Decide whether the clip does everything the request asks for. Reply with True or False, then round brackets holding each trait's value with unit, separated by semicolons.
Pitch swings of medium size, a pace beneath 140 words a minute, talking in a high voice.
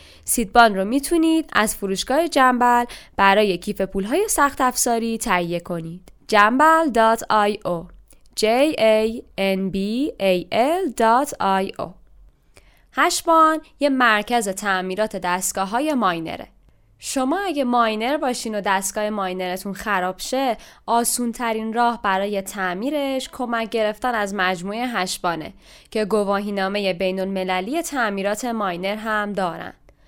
True (4.5 semitones; 110 wpm; 215 Hz)